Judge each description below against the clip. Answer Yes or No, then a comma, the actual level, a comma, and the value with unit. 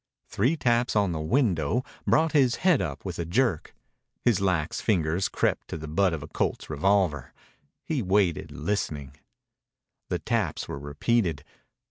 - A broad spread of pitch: Yes, wide, 7.2 semitones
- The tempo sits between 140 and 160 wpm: Yes, average, 150 wpm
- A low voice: Yes, very low, 95 Hz